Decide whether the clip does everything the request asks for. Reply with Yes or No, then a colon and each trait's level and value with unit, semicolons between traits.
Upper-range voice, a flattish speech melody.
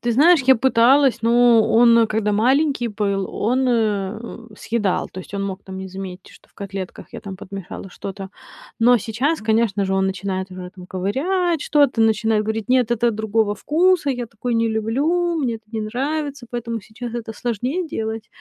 No: high, 225 Hz; average, 3.8 semitones